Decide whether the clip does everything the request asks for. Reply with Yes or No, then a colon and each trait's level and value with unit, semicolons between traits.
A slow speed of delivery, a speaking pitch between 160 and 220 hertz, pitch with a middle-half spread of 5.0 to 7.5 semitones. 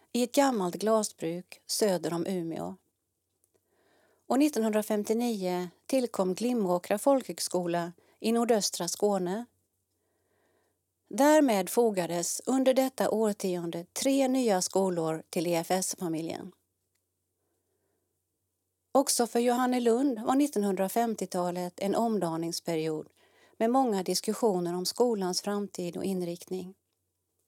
Yes: slow, 90 wpm; high, 190 Hz; average, 5.3 semitones